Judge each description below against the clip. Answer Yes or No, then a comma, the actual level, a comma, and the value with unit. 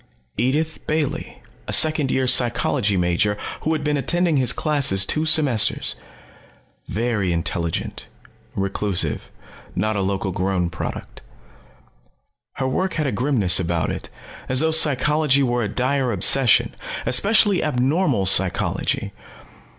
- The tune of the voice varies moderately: No, wide, 7.4 semitones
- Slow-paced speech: Yes, slow, 120 wpm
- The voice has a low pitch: Yes, low, 125 Hz